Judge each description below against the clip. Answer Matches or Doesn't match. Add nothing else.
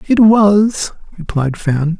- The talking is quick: Doesn't match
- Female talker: Doesn't match